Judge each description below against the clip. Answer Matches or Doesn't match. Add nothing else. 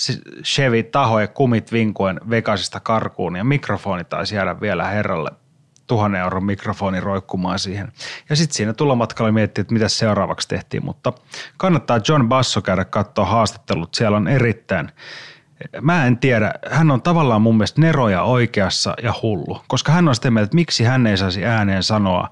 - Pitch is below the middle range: Matches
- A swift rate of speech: Matches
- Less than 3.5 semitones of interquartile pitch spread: Doesn't match